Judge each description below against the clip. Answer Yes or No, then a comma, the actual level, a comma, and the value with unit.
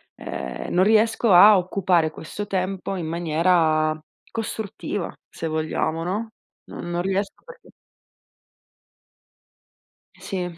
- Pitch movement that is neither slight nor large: Yes, average, 3.5 semitones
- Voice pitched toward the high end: No, medium, 180 Hz